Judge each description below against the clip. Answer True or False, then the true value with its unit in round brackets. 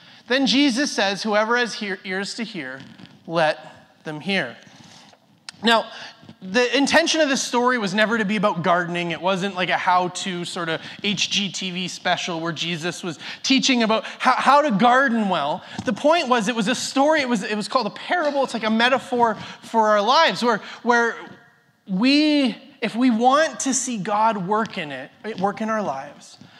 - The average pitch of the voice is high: True (220 Hz)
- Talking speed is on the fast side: False (180 wpm)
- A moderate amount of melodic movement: True (5.0 semitones)